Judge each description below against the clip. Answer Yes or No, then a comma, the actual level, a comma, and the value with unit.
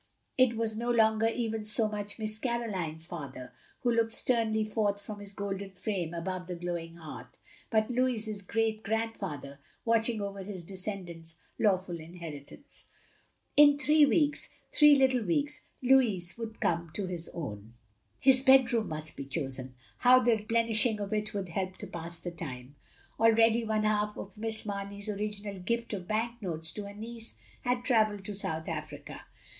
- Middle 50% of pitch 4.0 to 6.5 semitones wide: Yes, average, 4.6 semitones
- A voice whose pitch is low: No, high, 210 Hz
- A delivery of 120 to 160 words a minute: No, average, 170 wpm